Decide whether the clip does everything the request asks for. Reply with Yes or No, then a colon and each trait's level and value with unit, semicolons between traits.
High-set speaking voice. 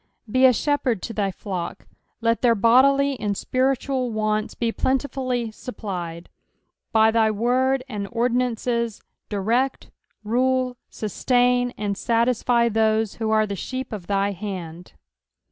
Yes: high, 230 Hz